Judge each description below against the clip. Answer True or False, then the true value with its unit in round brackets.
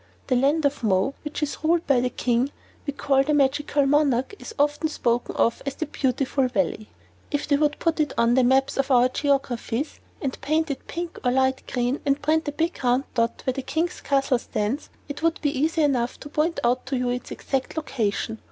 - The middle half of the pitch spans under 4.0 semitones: True (3.0 semitones)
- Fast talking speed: True (215 wpm)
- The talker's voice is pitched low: False (275 Hz)